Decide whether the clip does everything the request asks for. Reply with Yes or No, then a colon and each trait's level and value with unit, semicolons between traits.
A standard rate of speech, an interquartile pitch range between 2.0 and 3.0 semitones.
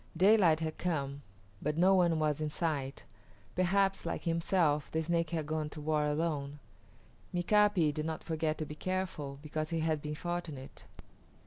Yes: average, 160 wpm; narrow, 2.5 semitones